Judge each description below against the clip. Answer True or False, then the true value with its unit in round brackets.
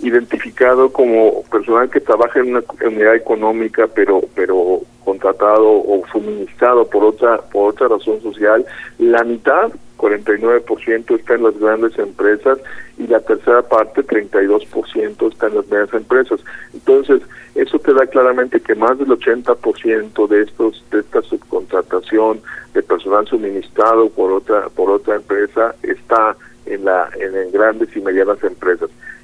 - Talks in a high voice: True (380 Hz)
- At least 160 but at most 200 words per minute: False (145 wpm)